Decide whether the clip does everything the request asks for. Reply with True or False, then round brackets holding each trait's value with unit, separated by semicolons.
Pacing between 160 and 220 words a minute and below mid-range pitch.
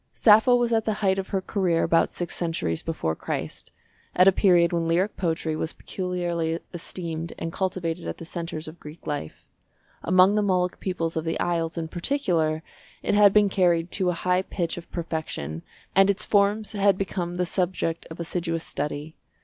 False (180 wpm; 175 Hz)